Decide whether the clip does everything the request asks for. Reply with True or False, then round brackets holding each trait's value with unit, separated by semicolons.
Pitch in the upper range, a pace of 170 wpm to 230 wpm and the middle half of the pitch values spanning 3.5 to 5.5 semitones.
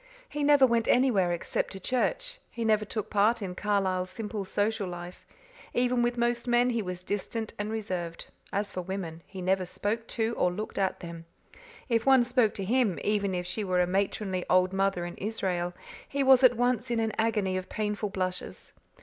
True (205 Hz; 190 wpm; 4.3 semitones)